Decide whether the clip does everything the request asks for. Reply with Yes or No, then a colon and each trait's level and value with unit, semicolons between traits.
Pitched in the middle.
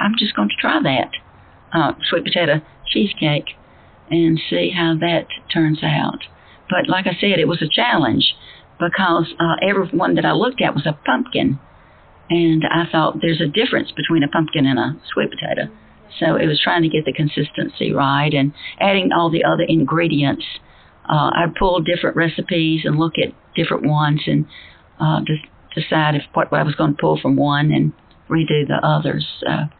Yes: medium, 160 Hz